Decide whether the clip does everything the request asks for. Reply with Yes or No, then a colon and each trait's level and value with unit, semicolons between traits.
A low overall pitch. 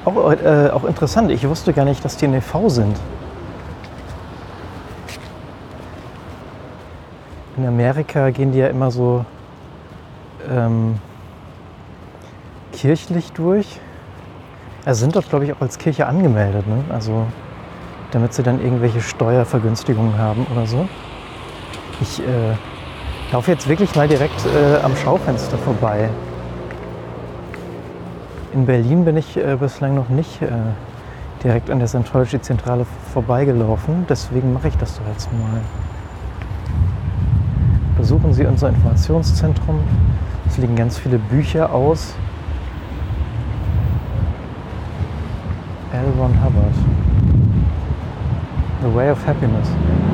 Yes: low, 115 Hz